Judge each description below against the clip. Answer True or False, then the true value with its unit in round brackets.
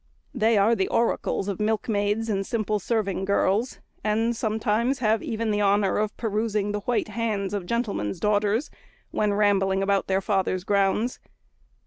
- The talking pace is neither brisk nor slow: True (150 wpm)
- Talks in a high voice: True (210 Hz)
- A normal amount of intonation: False (2.1 semitones)